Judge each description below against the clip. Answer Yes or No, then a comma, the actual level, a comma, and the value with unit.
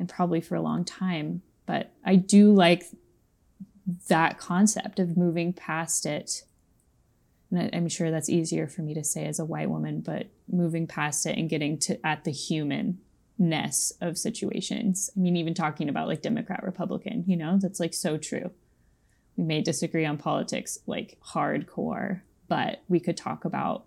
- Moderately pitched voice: Yes, medium, 175 Hz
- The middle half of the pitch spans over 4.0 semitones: No, average, 2.9 semitones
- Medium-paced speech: Yes, average, 170 wpm